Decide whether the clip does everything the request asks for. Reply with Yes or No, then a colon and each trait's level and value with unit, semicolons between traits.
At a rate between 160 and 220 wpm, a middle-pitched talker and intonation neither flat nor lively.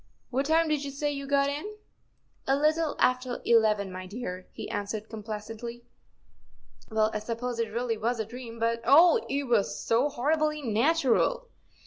No: average, 175 wpm; high, 245 Hz; average, 4.4 semitones